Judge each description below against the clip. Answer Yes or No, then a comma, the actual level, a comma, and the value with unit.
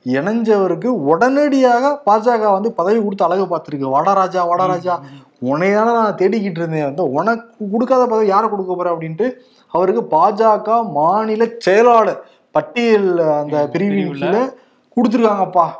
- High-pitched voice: Yes, high, 205 Hz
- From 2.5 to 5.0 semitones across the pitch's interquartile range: Yes, average, 4.6 semitones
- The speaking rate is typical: Yes, average, 115 wpm